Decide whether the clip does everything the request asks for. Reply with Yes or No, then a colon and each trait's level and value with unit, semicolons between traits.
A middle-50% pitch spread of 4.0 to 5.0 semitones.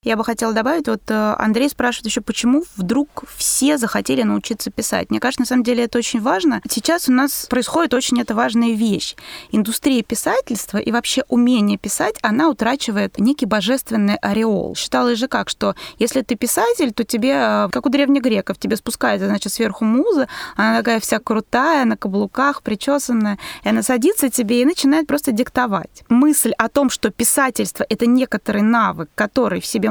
No: average, 3.1 semitones